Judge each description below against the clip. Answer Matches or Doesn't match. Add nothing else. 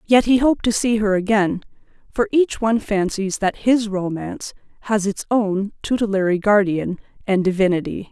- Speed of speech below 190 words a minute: Matches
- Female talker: Matches